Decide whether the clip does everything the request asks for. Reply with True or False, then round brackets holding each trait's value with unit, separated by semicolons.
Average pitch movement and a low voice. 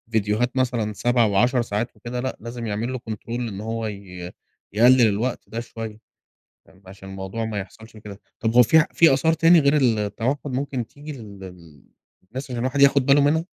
True (3.7 semitones; 115 Hz)